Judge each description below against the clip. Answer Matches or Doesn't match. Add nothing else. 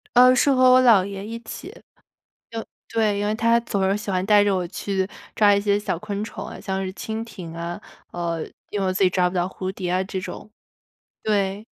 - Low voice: Doesn't match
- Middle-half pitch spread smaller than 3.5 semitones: Matches